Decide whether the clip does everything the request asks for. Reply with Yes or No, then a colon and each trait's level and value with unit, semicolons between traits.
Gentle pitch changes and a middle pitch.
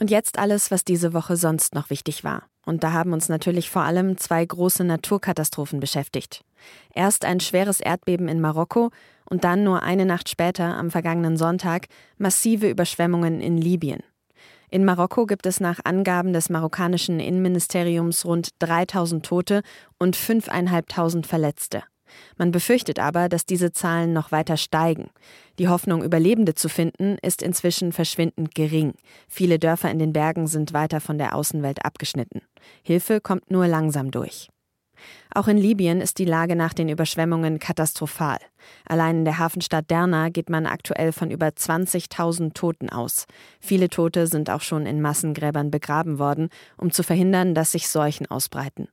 Yes: narrow, 2.2 semitones; medium, 170 Hz